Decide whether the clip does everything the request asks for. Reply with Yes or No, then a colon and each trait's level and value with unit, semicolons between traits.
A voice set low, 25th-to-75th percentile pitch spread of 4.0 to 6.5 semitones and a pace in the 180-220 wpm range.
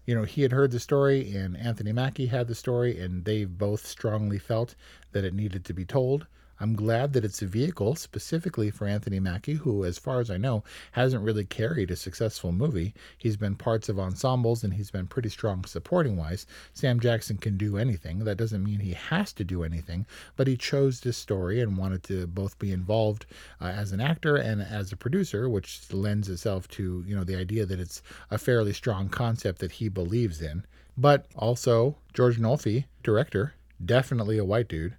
Yes: low, 110 Hz; average, 4.3 semitones; average, 200 wpm